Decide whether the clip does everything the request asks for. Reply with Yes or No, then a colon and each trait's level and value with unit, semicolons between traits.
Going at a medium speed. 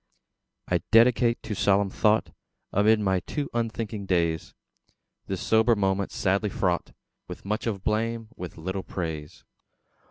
No: slow, 130 wpm